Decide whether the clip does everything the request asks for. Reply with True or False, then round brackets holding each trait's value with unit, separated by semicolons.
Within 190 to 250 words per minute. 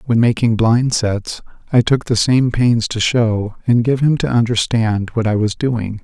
True (200 wpm)